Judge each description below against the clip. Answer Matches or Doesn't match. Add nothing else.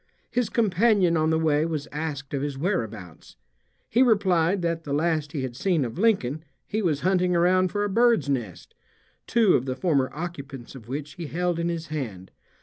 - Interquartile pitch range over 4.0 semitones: Matches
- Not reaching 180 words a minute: Doesn't match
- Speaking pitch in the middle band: Matches